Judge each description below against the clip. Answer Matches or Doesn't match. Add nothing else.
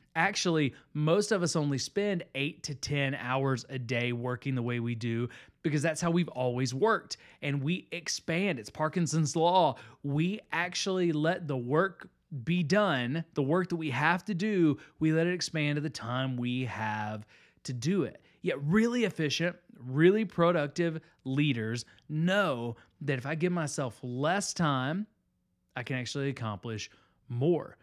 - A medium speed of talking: Matches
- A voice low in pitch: Doesn't match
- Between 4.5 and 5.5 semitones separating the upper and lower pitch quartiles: Matches